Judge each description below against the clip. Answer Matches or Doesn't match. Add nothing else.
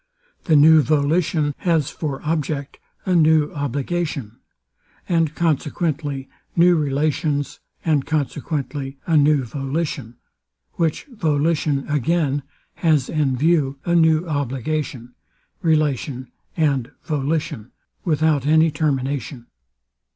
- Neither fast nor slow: Doesn't match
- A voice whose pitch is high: Doesn't match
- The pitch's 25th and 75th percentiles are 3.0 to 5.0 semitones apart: Doesn't match